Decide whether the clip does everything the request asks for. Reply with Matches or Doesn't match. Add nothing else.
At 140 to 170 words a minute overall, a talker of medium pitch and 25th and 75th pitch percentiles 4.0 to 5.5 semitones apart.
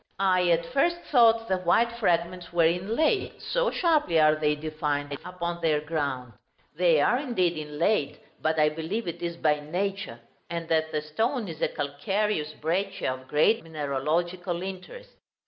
Matches